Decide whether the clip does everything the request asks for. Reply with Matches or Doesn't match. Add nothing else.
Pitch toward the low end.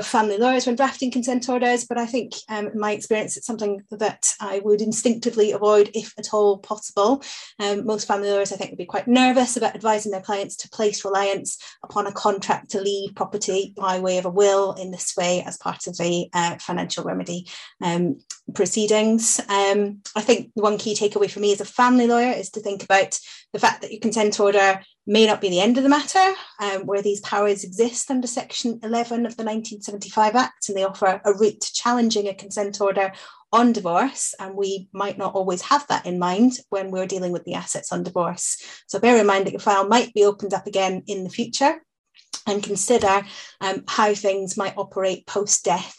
Doesn't match